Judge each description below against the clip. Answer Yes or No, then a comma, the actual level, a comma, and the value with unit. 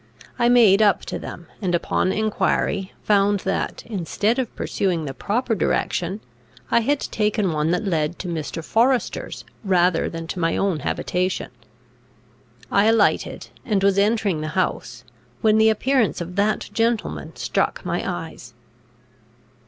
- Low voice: No, high, 195 Hz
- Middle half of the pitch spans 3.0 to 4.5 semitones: Yes, average, 4.1 semitones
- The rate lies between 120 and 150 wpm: Yes, average, 145 wpm